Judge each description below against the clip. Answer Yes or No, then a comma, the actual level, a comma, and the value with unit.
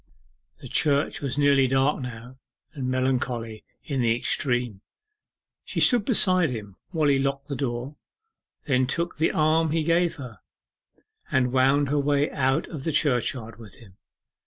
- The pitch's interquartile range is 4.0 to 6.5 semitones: No, average, 3.2 semitones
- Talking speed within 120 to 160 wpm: Yes, average, 155 wpm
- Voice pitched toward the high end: No, low, 135 Hz